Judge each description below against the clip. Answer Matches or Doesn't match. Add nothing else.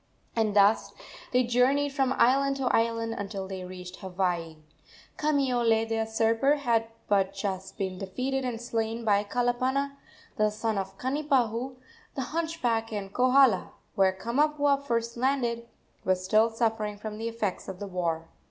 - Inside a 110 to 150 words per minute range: Matches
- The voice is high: Matches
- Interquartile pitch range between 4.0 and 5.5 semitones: Matches